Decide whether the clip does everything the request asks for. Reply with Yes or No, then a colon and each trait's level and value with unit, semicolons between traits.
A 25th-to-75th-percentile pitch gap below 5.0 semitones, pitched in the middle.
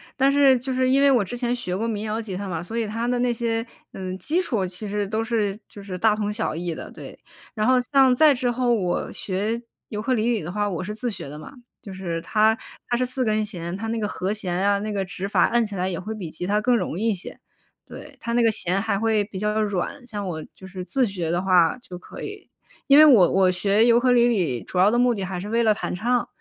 No: average, 4.2 semitones; high, 215 Hz